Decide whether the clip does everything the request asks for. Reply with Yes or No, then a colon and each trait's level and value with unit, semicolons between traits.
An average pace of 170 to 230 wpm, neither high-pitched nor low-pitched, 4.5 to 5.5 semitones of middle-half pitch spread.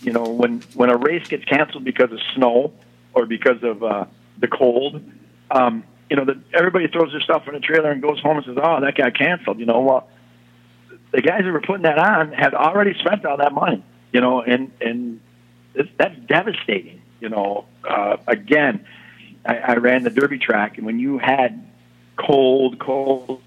No: average, 195 wpm; low, 130 Hz; average, 5.0 semitones